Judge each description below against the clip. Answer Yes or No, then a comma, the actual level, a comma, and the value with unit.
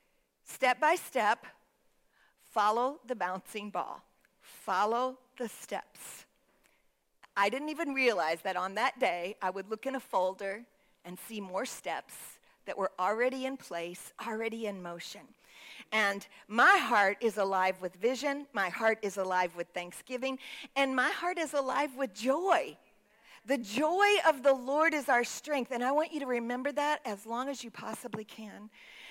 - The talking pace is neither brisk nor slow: Yes, average, 160 wpm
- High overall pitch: Yes, high, 235 Hz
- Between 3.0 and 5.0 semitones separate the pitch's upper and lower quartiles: No, wide, 5.4 semitones